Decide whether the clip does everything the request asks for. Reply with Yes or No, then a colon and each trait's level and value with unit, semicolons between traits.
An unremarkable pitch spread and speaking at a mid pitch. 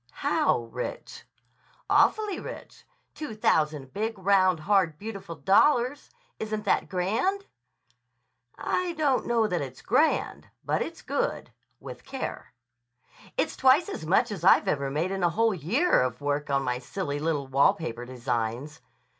No: wide, 7.8 semitones; medium, 180 Hz